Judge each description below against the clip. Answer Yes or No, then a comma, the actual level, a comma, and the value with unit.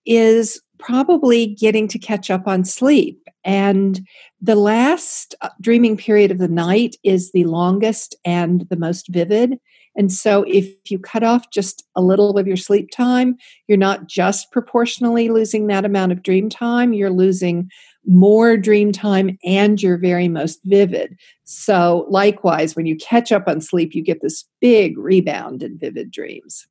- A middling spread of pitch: Yes, average, 3.5 semitones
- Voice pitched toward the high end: Yes, high, 200 Hz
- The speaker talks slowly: No, average, 160 wpm